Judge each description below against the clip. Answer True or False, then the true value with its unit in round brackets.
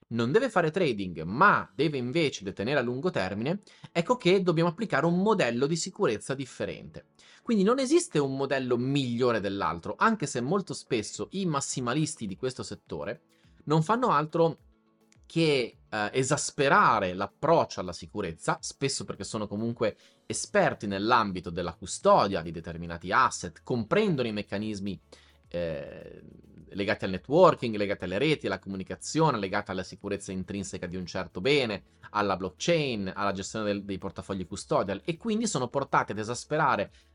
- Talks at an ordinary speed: True (145 wpm)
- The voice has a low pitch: True (120 Hz)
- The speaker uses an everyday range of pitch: False (8.7 semitones)